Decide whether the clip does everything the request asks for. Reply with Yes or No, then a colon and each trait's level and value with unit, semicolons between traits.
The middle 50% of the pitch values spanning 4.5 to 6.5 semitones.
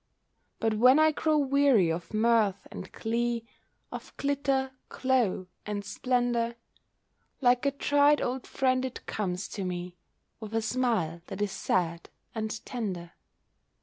Yes: average, 4.8 semitones